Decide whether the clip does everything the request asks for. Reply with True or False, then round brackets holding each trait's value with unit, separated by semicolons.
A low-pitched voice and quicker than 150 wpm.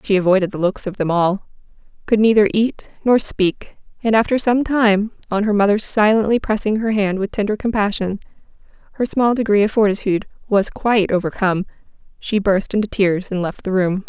False (205 Hz; 180 wpm)